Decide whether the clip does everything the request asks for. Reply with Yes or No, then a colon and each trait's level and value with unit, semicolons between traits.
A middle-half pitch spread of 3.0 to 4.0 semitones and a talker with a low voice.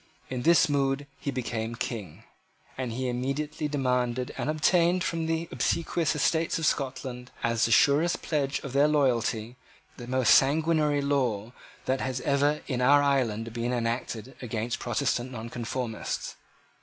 Yes: average, 3.4 semitones; low, 130 Hz